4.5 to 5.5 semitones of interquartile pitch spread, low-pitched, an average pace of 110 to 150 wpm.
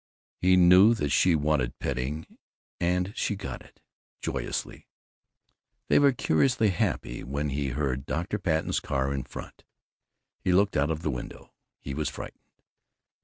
Yes: average, 5.0 semitones; very low, 75 Hz; average, 145 wpm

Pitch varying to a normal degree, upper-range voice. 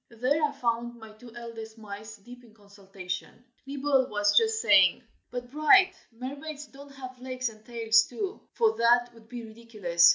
Yes: average, 3.7 semitones; high, 240 Hz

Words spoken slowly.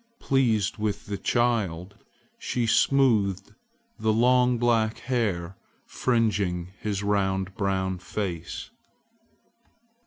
Yes: slow, 90 wpm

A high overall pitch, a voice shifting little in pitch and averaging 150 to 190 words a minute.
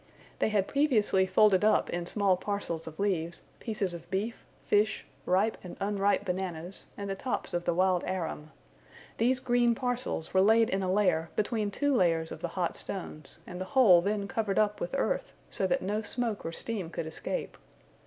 No: high, 195 Hz; average, 3.5 semitones; average, 185 wpm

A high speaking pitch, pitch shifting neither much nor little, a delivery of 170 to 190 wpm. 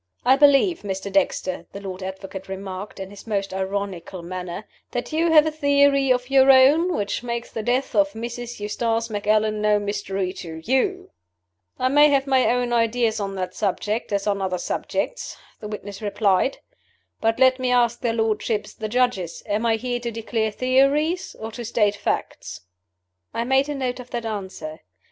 Yes: high, 225 Hz; average, 4.3 semitones; average, 175 wpm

